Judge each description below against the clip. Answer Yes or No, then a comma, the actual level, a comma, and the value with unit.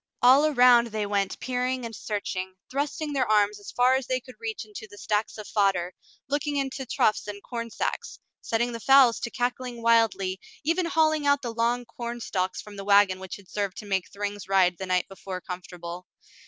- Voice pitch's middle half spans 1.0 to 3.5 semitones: No, average, 4.3 semitones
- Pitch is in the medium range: No, high, 225 Hz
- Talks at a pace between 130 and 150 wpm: No, average, 195 wpm